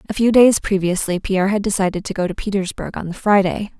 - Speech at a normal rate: No, fast, 220 wpm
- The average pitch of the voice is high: Yes, high, 195 Hz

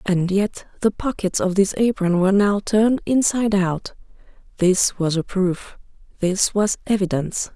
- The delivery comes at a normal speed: Yes, average, 150 wpm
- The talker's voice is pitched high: Yes, high, 195 Hz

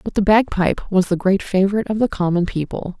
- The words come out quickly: Yes, fast, 220 wpm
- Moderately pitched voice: No, high, 195 Hz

